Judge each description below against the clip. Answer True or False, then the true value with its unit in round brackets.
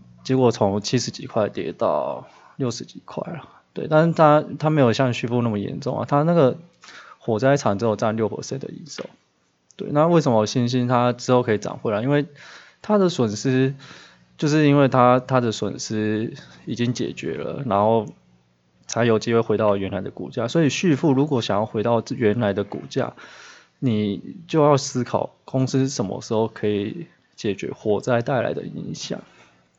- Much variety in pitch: False (4.4 semitones)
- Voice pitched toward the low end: True (120 Hz)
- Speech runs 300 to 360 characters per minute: False (260 characters per minute)